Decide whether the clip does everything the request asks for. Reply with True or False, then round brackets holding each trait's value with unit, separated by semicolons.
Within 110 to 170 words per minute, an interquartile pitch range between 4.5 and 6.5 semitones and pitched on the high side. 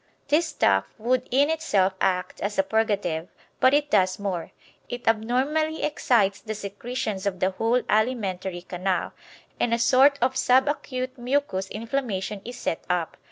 True (155 wpm; 5.2 semitones; 225 Hz)